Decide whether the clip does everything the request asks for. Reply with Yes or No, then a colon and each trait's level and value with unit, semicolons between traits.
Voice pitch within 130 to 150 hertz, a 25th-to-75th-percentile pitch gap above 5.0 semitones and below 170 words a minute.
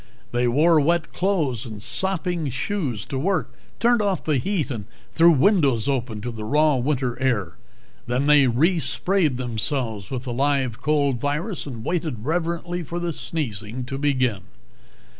Yes: medium, 140 Hz; wide, 5.6 semitones; average, 155 wpm